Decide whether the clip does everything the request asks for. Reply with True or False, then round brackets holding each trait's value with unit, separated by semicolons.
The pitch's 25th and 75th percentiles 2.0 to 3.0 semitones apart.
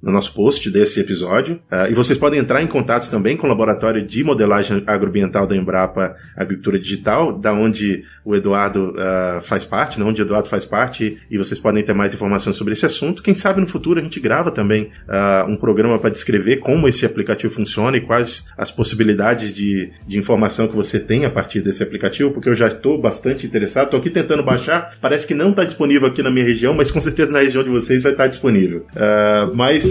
False (5.1 semitones)